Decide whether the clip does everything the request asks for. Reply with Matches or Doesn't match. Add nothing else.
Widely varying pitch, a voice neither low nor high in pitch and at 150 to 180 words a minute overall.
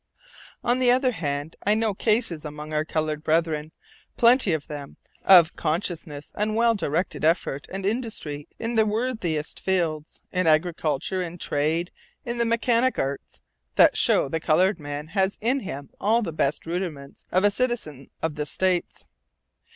Matches